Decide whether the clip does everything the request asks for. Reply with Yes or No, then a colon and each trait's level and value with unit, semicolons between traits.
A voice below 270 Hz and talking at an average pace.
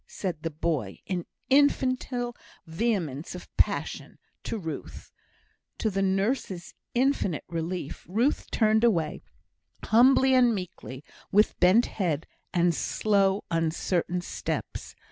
No: high, 190 Hz; slow, 110 wpm